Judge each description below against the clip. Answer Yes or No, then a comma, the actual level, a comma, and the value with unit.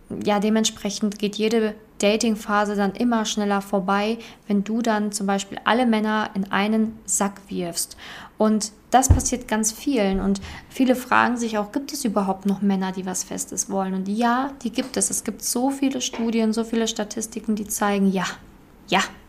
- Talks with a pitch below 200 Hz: No, high, 215 Hz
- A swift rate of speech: No, average, 175 wpm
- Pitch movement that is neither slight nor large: No, narrow, 2.3 semitones